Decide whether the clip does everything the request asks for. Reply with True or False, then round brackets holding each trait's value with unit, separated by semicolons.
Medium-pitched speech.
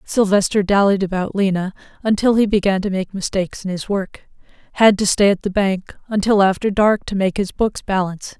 False (195 Hz)